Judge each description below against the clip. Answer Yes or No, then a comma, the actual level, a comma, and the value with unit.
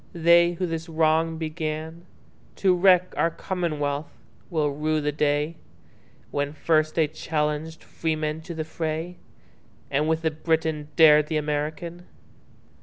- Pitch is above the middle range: No, medium, 160 Hz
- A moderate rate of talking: No, slow, 115 wpm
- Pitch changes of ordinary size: No, narrow, 1.6 semitones